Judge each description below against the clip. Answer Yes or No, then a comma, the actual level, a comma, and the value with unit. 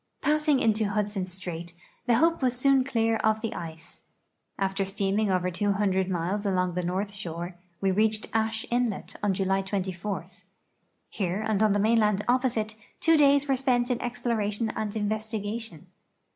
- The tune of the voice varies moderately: Yes, average, 3.3 semitones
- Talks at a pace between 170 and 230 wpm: No, average, 155 wpm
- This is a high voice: Yes, high, 210 Hz